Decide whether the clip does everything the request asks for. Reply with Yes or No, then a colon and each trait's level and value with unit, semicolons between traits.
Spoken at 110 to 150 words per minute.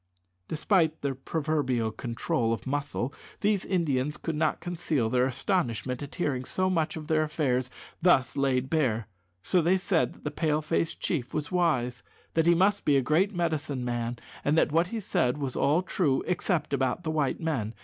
No: average, 180 wpm